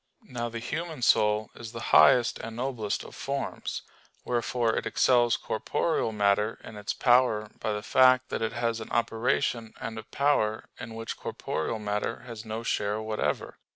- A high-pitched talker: No, low, 115 Hz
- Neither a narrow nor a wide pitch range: No, narrow, 2.2 semitones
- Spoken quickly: No, average, 165 wpm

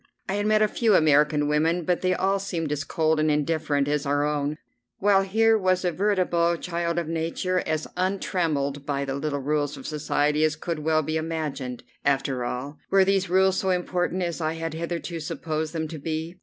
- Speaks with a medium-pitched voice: Yes, medium, 160 Hz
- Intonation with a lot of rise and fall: No, average, 3.5 semitones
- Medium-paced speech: Yes, average, 195 wpm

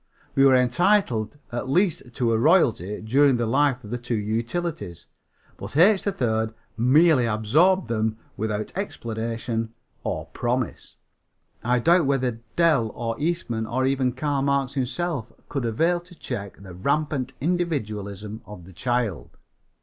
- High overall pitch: No, low, 125 Hz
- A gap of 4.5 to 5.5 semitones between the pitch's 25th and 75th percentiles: Yes, average, 5.0 semitones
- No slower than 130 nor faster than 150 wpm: Yes, average, 140 wpm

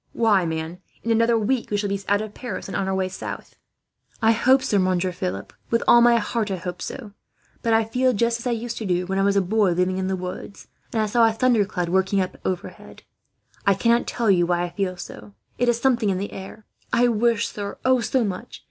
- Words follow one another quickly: Yes, fast, 235 wpm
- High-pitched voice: Yes, high, 205 Hz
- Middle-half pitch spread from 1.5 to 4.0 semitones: Yes, average, 3.7 semitones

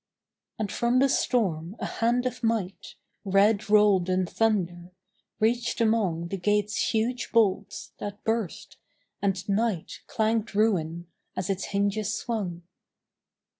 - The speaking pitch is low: No, high, 205 Hz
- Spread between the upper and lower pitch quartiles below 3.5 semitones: Yes, average, 3.1 semitones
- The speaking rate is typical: No, slow, 125 wpm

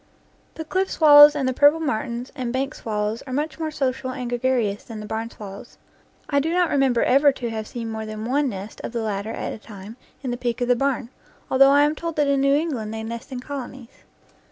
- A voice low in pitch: No, very high, 255 Hz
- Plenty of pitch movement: No, average, 4.2 semitones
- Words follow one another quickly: Yes, fast, 230 wpm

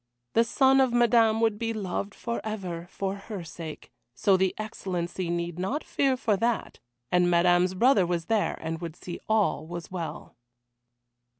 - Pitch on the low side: No, high, 190 Hz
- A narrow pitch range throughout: No, average, 4.6 semitones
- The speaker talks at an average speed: Yes, average, 160 wpm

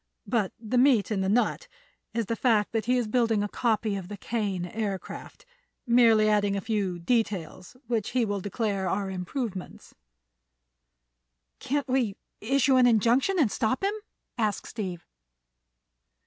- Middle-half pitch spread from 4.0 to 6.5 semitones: No, average, 3.6 semitones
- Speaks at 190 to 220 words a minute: No, average, 150 wpm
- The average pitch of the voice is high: Yes, high, 220 Hz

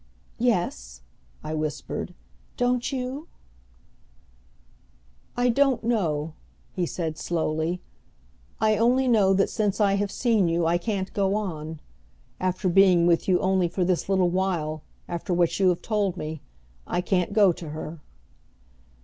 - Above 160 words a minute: No, average, 140 wpm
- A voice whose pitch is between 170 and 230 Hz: Yes, medium, 185 Hz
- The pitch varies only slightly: No, average, 3.9 semitones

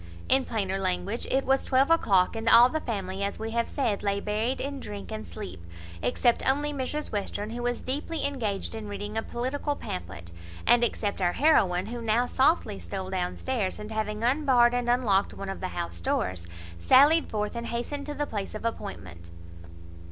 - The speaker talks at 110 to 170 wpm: No, average, 190 wpm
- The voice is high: Yes, high, 220 Hz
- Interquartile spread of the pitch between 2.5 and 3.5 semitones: No, average, 4.8 semitones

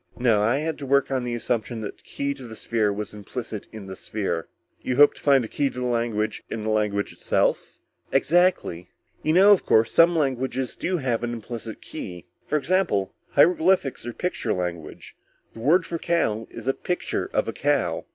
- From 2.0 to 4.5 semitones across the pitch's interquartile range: No, average, 5.3 semitones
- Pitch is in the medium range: No, low, 120 Hz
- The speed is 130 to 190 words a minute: No, average, 200 wpm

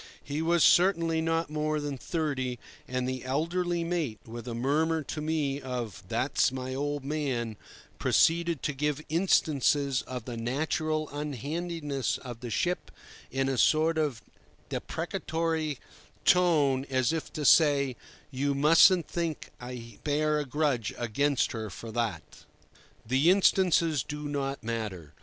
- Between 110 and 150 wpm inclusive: Yes, average, 140 wpm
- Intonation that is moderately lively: Yes, average, 3.9 semitones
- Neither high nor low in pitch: Yes, medium, 145 Hz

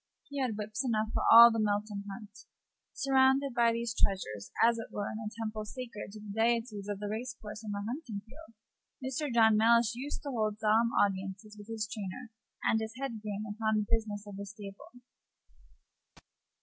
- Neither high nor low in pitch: No, high, 220 Hz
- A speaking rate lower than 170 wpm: No, average, 190 wpm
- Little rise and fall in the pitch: Yes, narrow, 2.2 semitones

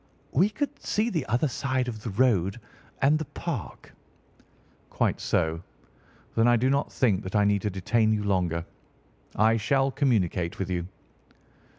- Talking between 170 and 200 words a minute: No, average, 160 wpm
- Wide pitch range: Yes, wide, 5.9 semitones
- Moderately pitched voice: No, low, 110 Hz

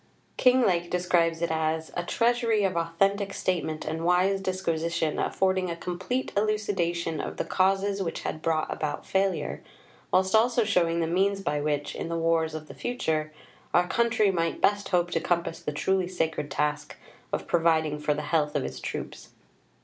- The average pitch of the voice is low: No, medium, 175 Hz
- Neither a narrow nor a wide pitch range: Yes, average, 3.3 semitones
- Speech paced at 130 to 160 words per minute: No, average, 170 wpm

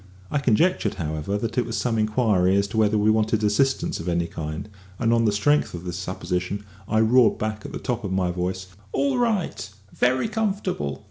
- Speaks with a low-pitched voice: Yes, low, 110 Hz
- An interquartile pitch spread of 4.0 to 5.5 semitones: Yes, average, 5.2 semitones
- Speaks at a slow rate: No, average, 200 wpm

